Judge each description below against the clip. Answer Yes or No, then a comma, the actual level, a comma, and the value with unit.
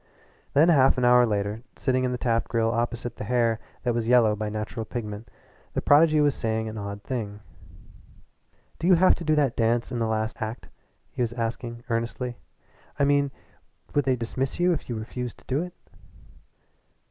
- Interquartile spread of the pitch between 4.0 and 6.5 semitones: No, average, 3.0 semitones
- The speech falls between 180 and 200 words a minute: Yes, average, 185 wpm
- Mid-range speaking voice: No, low, 120 Hz